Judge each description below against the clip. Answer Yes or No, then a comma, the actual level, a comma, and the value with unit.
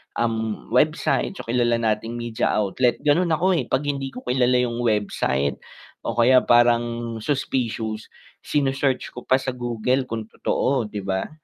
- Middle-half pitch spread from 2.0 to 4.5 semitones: Yes, narrow, 2.6 semitones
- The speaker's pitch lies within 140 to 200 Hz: No, low, 120 Hz